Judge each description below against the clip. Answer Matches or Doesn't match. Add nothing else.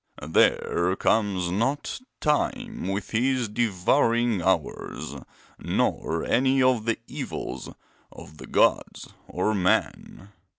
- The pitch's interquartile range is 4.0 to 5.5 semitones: Matches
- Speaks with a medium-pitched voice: Doesn't match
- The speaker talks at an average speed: Doesn't match